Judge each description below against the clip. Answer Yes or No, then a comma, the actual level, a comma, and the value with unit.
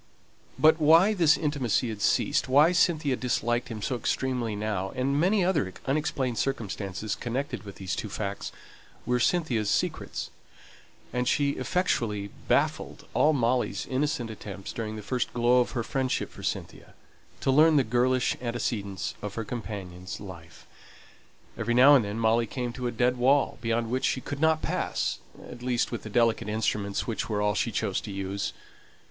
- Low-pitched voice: Yes, low, 120 Hz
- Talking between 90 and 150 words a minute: No, average, 165 wpm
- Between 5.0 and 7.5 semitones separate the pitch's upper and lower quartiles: No, average, 4.3 semitones